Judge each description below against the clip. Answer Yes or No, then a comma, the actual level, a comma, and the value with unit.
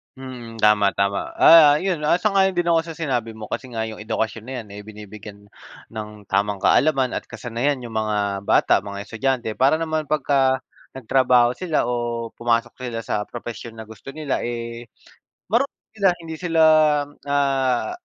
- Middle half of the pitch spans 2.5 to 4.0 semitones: No, average, 4.6 semitones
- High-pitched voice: No, low, 120 Hz